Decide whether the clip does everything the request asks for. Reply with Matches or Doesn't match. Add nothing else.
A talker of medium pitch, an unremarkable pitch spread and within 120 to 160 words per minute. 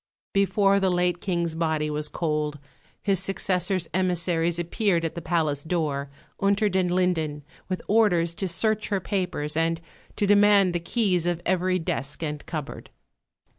Matches